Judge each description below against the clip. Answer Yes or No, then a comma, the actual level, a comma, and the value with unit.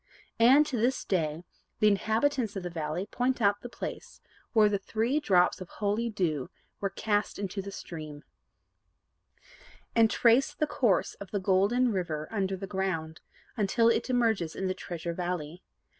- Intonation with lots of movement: No, average, 4.3 semitones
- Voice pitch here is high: Yes, high, 200 Hz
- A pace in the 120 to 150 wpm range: No, average, 160 wpm